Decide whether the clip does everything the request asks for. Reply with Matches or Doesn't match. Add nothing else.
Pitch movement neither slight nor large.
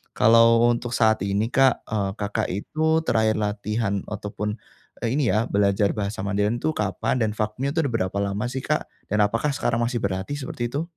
Matches